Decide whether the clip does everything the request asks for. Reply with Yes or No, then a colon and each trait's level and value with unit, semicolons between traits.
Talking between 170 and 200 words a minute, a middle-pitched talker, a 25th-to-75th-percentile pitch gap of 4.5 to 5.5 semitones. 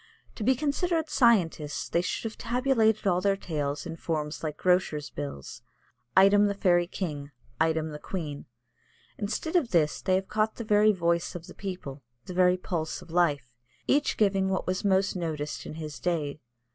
Yes: average, 175 wpm; medium, 180 Hz; average, 4.8 semitones